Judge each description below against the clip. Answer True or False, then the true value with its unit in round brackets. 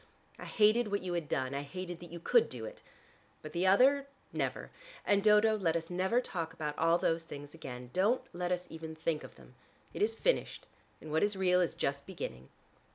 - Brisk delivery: True (210 wpm)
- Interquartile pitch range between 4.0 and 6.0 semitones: True (4.3 semitones)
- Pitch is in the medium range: True (175 Hz)